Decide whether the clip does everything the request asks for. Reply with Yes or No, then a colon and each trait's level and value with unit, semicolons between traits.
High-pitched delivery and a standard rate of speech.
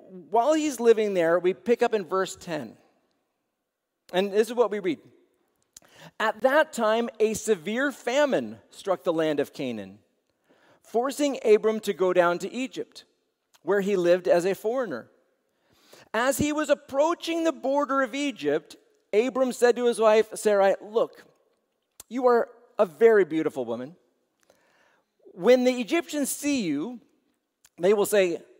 Yes: high, 230 Hz; average, 145 wpm